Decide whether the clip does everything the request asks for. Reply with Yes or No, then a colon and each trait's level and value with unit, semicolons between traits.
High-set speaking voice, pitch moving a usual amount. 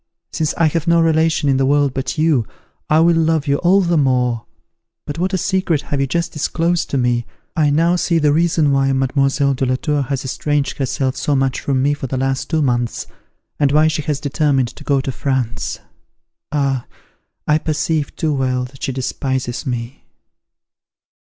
No: medium, 140 Hz; average, 3.0 semitones